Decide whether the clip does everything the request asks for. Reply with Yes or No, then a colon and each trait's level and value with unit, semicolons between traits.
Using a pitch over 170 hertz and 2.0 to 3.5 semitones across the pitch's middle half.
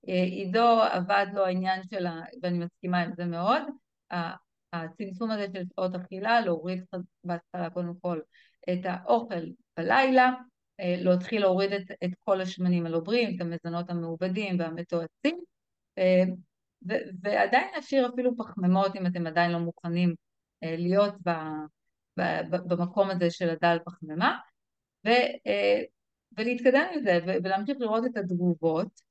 Yes: medium, 185 Hz; average, 3.1 semitones